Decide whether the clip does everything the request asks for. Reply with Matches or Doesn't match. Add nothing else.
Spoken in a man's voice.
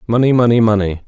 Matches